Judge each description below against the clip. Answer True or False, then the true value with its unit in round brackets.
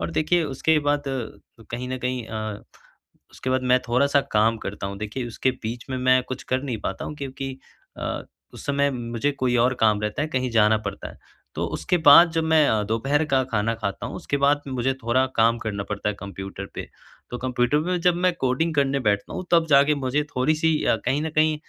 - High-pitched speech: False (130 Hz)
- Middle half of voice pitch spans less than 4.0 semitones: False (4.3 semitones)